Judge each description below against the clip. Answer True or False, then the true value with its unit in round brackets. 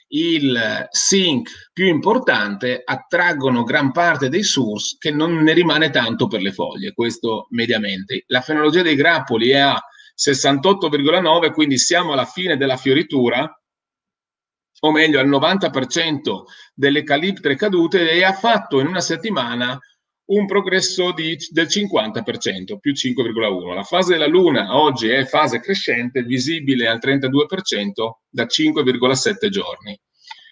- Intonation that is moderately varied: False (6.3 semitones)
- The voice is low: False (155 Hz)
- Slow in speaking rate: False (130 wpm)